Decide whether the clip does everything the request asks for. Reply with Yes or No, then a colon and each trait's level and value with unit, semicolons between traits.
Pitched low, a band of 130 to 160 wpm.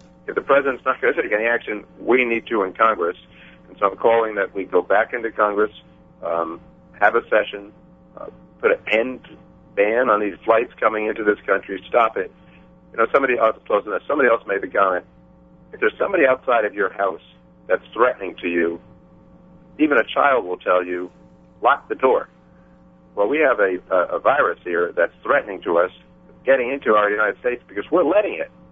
No: very low, 85 Hz; average, 195 wpm